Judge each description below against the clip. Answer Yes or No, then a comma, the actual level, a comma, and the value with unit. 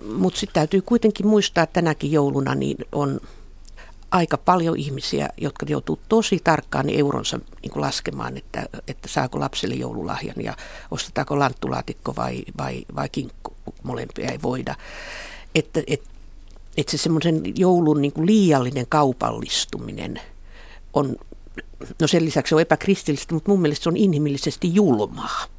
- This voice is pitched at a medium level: Yes, medium, 155 Hz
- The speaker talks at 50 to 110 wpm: No, average, 135 wpm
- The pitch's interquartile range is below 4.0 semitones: No, average, 4.3 semitones